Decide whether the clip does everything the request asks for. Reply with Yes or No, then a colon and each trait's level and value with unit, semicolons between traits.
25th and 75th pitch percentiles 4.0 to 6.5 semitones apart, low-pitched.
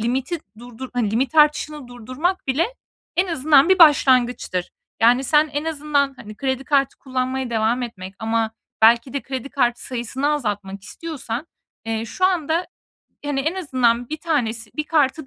No: average, 4.3 semitones; very high, 265 Hz